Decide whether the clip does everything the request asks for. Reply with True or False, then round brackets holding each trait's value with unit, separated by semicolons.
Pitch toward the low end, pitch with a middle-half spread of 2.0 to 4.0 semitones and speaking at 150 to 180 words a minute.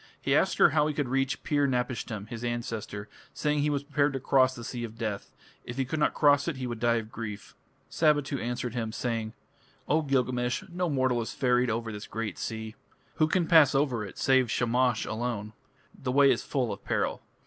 False (125 Hz; 3.7 semitones; 205 wpm)